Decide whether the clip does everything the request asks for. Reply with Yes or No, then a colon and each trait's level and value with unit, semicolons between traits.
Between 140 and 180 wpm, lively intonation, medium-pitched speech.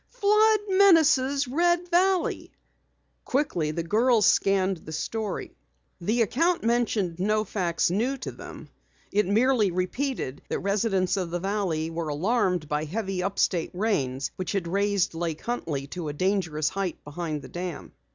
No: average, 150 wpm; wide, 6.2 semitones; high, 195 Hz